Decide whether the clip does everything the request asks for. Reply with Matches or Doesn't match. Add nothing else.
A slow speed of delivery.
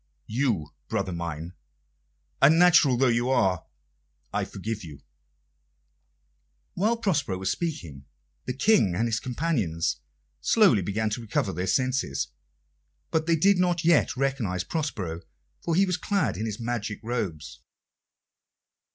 Matches